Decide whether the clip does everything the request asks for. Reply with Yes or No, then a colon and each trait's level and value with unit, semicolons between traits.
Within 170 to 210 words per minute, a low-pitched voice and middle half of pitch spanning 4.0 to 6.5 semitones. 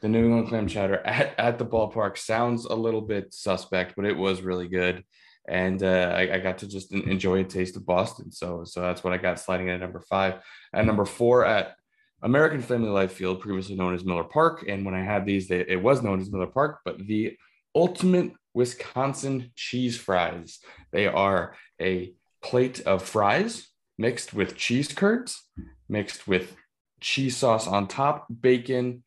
Yes: average, 185 wpm; low, 100 Hz; average, 4.9 semitones